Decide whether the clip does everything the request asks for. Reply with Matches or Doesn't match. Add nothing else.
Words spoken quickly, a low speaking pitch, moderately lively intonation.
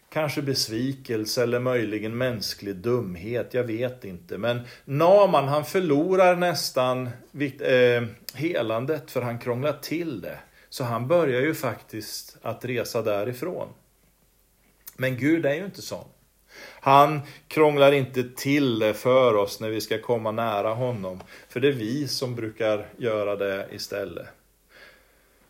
Doesn't match